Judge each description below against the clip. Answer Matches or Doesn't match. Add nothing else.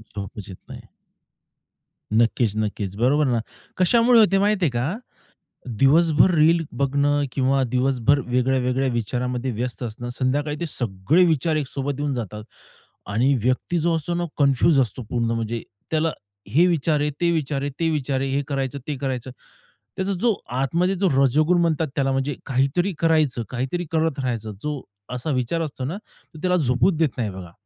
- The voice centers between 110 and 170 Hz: Matches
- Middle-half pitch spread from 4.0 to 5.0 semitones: Matches